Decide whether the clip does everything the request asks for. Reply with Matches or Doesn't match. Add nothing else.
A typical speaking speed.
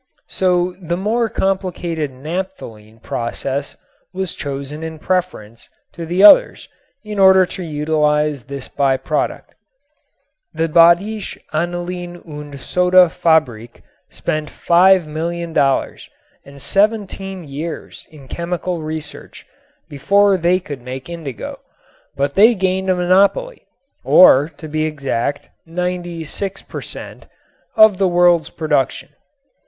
Doesn't match